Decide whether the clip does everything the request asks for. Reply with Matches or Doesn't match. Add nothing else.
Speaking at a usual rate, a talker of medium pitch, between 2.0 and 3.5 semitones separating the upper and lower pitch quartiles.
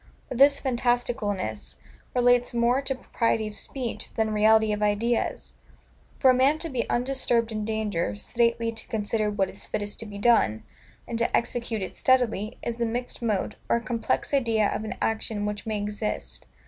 Doesn't match